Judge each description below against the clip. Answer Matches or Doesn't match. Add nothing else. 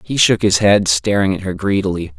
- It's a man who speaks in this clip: Matches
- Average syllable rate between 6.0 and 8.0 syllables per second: Doesn't match